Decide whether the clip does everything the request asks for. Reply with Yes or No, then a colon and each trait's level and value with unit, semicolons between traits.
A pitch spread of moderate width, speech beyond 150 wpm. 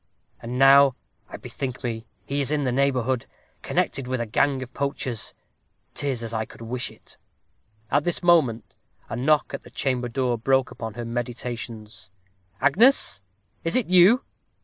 Yes: average, 3.1 semitones; average, 160 wpm